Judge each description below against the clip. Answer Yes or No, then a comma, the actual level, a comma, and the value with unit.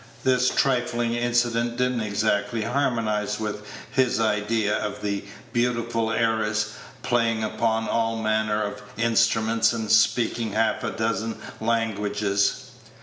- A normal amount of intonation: No, narrow, 1.7 semitones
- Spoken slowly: Yes, slow, 120 wpm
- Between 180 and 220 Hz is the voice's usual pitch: No, low, 115 Hz